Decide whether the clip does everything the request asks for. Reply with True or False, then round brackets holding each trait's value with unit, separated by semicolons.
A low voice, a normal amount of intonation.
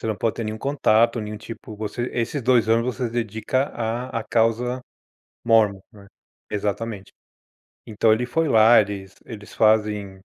False (110 Hz; 1.9 semitones)